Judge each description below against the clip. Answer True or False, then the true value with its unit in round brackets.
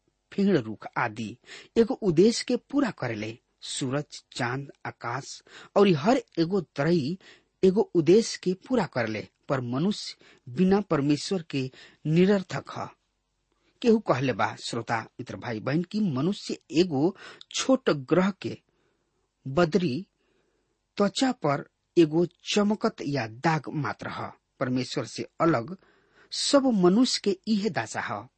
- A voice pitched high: False (175 Hz)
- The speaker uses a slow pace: True (120 wpm)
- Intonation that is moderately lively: False (8.5 semitones)